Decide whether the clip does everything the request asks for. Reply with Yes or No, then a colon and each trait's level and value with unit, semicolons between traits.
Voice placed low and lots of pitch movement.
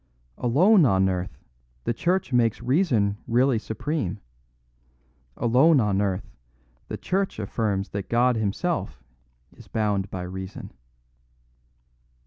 Yes: low, 110 Hz; wide, 5.8 semitones